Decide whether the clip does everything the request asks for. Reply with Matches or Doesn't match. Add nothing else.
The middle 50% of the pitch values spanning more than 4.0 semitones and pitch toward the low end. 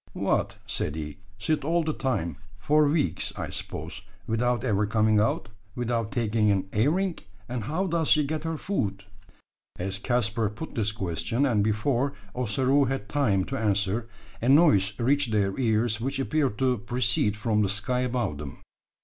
Matches